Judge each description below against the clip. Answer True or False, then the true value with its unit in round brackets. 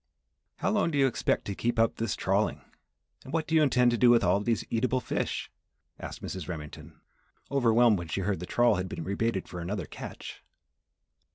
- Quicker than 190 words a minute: True (200 wpm)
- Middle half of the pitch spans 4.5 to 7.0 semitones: True (5.2 semitones)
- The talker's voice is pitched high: False (115 Hz)